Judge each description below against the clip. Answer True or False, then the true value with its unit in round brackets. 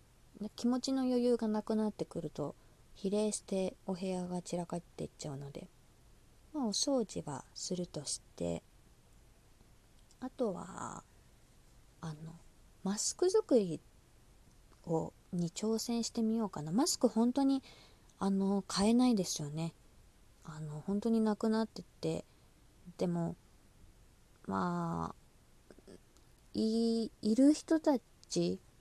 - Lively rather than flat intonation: True (8.4 semitones)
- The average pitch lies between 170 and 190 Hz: True (185 Hz)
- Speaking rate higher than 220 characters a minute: False (215 characters per minute)